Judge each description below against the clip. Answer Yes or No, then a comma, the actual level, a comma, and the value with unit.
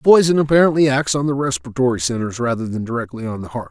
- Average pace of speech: No, fast, 225 wpm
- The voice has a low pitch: Yes, low, 130 Hz